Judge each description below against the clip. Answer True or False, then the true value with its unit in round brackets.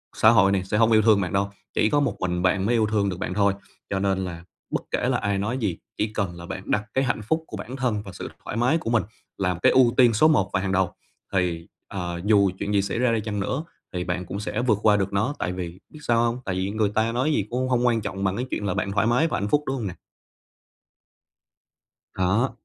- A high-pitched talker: False (105 Hz)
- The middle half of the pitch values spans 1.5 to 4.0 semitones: True (3.7 semitones)